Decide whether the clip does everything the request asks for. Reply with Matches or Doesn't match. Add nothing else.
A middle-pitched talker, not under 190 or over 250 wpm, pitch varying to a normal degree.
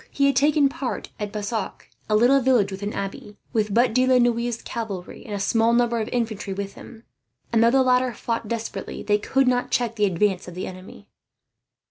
Doesn't match